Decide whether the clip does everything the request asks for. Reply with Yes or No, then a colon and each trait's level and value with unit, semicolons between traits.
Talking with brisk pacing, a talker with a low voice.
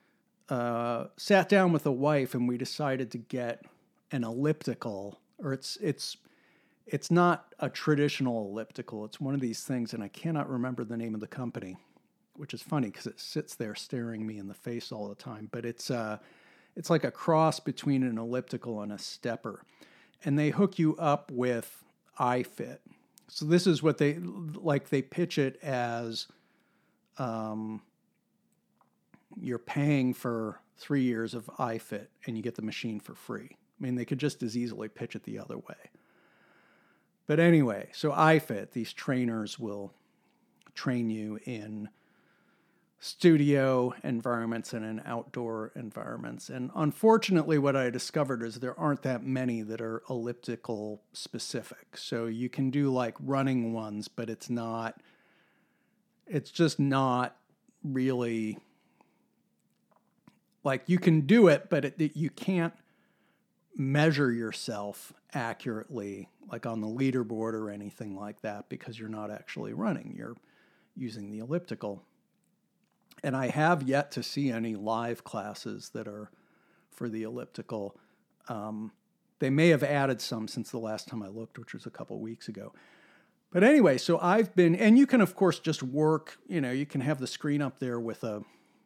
No: average, 160 wpm; low, 125 Hz